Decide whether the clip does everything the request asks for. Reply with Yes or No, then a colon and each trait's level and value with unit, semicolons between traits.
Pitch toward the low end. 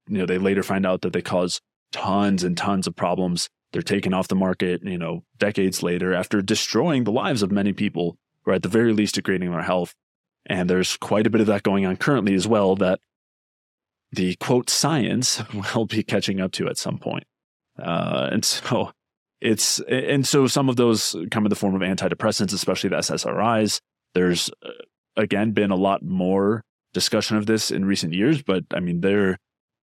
Yes: very low, 95 Hz